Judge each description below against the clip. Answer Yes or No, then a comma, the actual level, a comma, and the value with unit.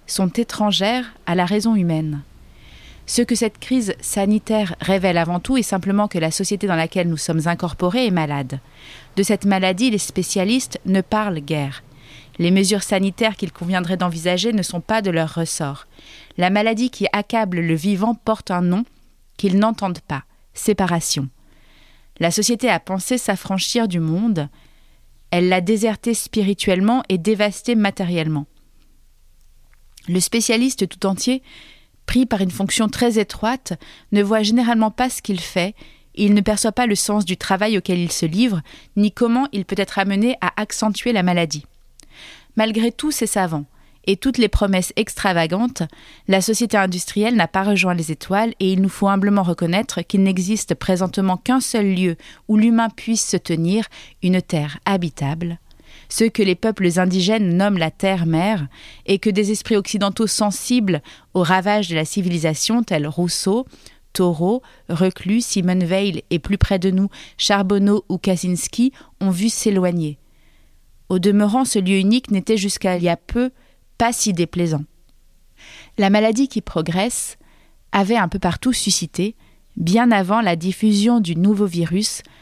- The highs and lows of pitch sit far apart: No, average, 3.7 semitones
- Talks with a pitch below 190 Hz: No, high, 195 Hz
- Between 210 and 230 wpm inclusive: No, average, 160 wpm